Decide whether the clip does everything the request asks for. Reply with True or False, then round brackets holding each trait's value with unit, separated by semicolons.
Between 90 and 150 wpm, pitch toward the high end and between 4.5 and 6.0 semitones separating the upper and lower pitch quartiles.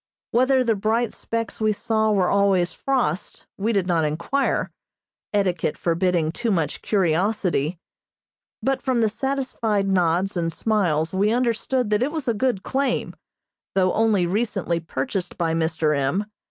True (145 wpm; 200 Hz; 5.0 semitones)